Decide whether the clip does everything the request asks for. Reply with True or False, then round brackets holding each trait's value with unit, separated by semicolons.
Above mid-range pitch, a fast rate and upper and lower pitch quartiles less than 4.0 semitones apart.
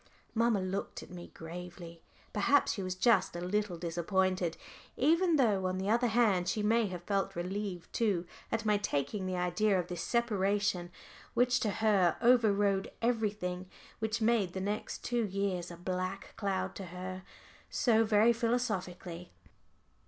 False (195 Hz; 155 wpm; 3.4 semitones)